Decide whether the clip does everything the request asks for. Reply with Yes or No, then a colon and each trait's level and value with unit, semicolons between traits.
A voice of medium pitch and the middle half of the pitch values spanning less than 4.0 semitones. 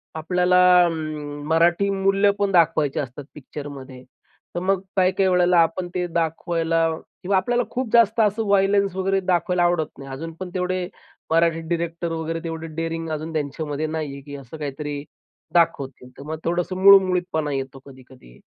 Yes: medium, 165 Hz; average, 3.6 semitones